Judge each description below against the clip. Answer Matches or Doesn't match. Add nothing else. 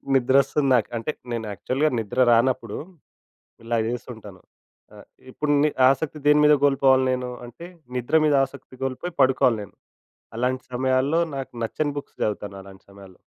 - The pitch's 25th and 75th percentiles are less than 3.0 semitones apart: Doesn't match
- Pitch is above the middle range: Doesn't match